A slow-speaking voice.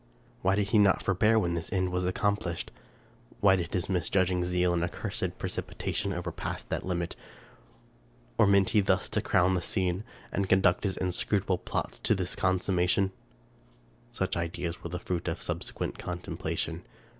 No: average, 155 wpm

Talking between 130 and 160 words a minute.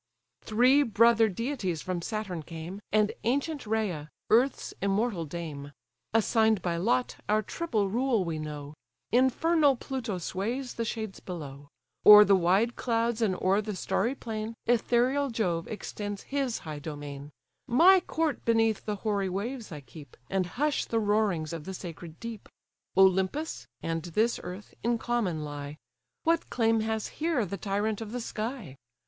Yes: average, 150 wpm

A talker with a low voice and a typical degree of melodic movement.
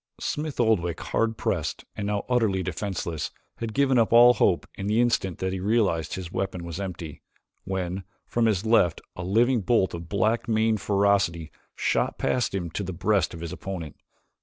Yes: low, 100 Hz; average, 4.1 semitones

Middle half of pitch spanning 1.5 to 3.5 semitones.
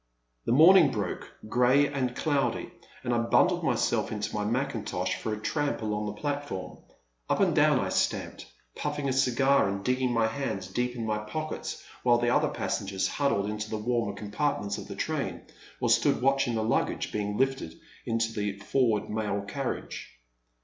No: average, 4.3 semitones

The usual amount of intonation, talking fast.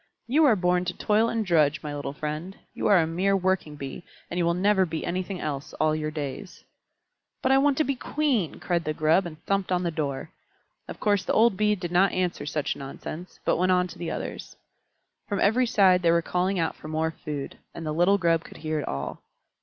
Yes: average, 4.1 semitones; fast, 225 wpm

